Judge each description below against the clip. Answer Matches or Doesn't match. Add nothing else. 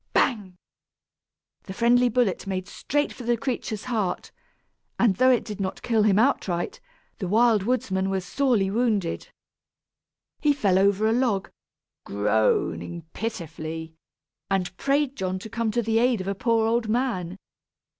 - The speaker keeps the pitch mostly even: Doesn't match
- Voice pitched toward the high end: Matches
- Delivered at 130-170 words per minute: Matches